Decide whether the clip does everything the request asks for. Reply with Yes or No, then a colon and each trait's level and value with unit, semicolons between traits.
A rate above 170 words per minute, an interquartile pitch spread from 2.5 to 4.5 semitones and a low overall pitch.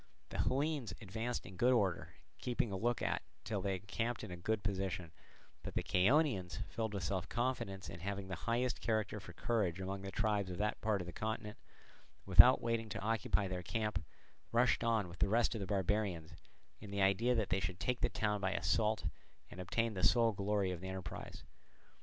Yes: average, 200 wpm; average, 3.3 semitones; low, 100 Hz